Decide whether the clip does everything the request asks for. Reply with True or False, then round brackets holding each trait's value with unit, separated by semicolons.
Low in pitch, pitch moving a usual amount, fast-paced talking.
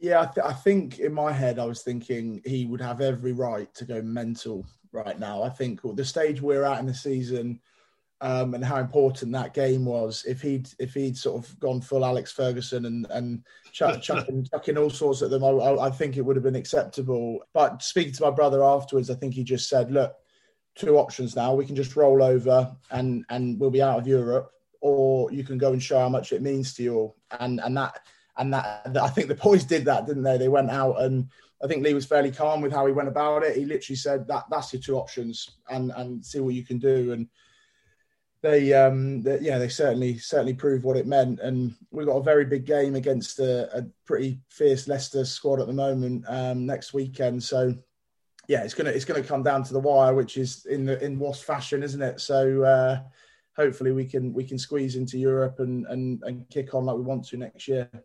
False (130 Hz; 1.7 semitones; 225 wpm)